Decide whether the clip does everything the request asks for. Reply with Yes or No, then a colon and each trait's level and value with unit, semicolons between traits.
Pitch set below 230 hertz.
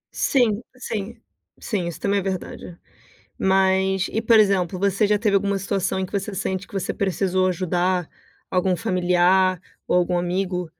Yes: high, 190 Hz